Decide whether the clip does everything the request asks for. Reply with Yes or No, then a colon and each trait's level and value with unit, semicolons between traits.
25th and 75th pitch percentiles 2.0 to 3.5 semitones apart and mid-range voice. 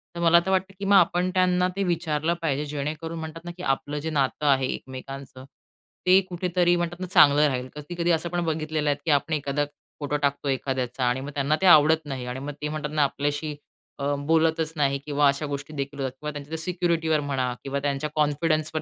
Yes: average, 2.9 semitones; medium, 150 Hz